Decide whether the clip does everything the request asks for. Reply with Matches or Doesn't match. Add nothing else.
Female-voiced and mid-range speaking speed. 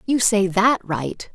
Matches